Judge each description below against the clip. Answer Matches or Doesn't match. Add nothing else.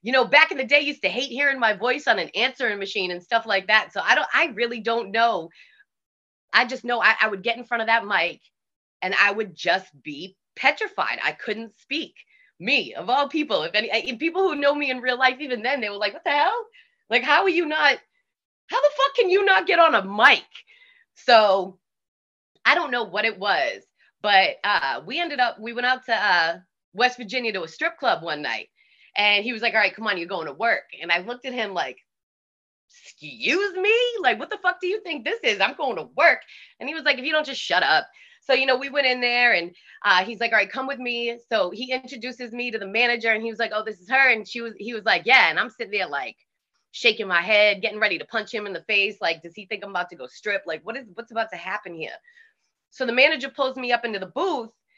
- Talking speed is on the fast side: Matches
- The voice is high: Matches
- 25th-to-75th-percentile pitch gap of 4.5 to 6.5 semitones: Matches